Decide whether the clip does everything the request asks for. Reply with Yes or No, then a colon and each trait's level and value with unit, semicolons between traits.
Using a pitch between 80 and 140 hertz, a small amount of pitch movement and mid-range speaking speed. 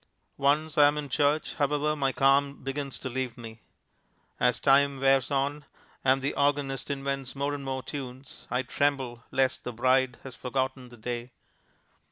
Yes: low, 135 Hz; narrow, 1.6 semitones; average, 165 wpm